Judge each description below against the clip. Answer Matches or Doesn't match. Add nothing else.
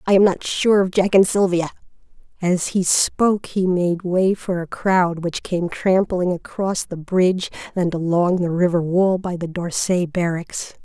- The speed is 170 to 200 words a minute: Matches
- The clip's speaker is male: Doesn't match